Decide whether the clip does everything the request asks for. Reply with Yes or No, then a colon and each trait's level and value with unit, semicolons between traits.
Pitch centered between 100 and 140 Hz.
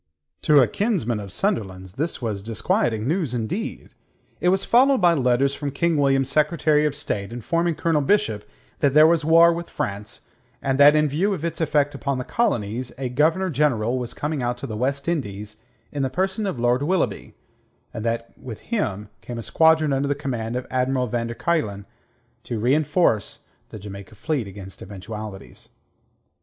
Yes: low, 135 Hz